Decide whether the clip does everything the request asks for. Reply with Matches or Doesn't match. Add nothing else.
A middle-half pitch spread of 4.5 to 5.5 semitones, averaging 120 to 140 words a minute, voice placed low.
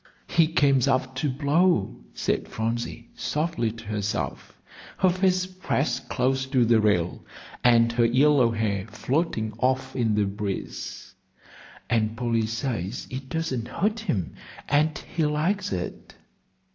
Matches